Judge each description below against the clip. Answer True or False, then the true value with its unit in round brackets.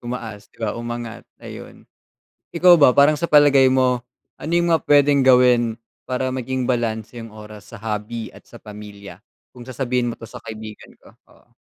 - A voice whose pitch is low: True (120 Hz)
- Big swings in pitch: False (3.1 semitones)